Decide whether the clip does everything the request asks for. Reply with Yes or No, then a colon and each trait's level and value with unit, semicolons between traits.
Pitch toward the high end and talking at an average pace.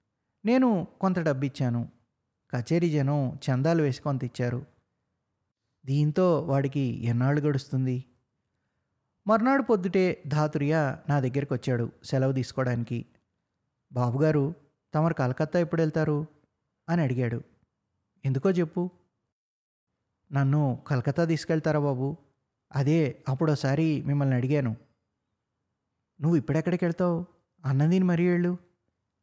No: medium, 140 Hz; average, 90 wpm